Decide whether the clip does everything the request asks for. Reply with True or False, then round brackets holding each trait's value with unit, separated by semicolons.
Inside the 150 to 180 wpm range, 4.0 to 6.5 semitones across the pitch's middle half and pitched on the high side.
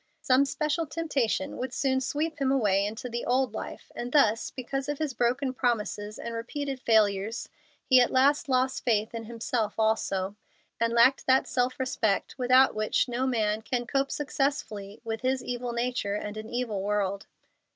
False (170 wpm; 3.3 semitones; 245 Hz)